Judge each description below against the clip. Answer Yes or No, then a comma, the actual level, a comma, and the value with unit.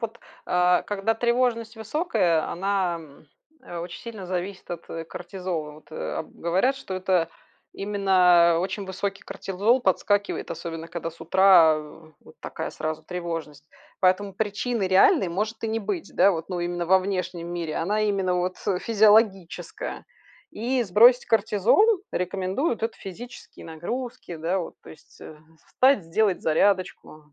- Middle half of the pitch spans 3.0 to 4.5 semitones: Yes, average, 3.8 semitones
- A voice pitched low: No, high, 190 Hz